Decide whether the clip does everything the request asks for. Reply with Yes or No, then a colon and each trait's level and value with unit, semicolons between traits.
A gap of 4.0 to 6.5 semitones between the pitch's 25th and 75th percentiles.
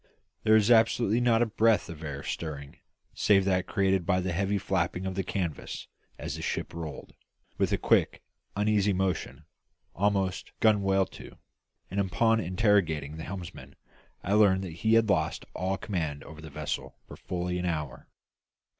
No: average, 3.5 semitones